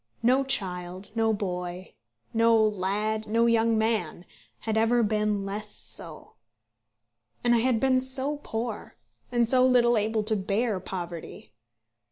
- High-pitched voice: Yes, high, 220 Hz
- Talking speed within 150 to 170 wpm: No, slow, 135 wpm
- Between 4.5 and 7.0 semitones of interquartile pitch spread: No, average, 3.1 semitones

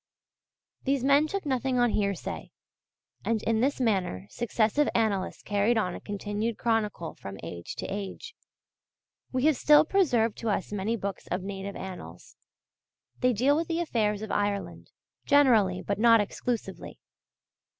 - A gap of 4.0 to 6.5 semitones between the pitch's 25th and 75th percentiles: Yes, average, 4.4 semitones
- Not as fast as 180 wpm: Yes, average, 145 wpm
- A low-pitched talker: No, high, 225 Hz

